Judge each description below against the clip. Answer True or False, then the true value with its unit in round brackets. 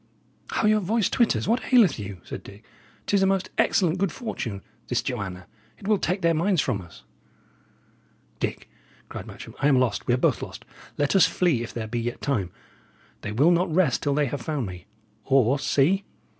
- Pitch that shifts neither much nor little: False (8.4 semitones)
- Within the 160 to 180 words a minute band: False (195 wpm)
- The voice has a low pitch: False (145 Hz)